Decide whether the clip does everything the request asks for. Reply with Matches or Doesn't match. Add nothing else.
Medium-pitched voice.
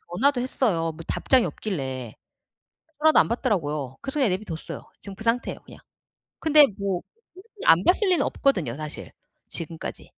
Doesn't match